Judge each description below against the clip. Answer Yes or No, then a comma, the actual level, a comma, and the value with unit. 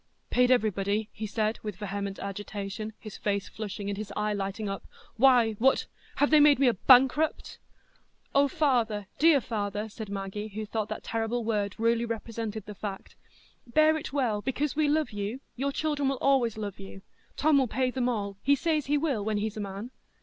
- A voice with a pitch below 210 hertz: No, high, 220 Hz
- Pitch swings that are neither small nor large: Yes, average, 4.5 semitones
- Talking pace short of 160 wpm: No, average, 185 wpm